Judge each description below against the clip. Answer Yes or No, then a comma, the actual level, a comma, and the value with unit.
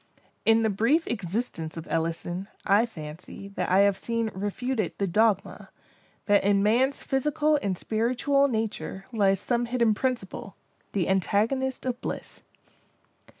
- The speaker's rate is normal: No, slow, 130 wpm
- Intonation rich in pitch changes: No, average, 4.1 semitones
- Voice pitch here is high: Yes, high, 215 Hz